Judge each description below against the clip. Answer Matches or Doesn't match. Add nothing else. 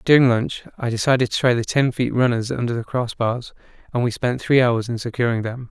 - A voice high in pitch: Doesn't match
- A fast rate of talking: Matches